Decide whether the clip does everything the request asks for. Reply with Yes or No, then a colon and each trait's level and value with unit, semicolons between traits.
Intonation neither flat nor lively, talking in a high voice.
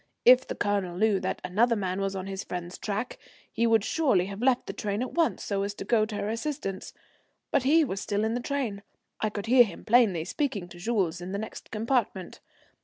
Yes: average, 3.8 semitones; high, 210 Hz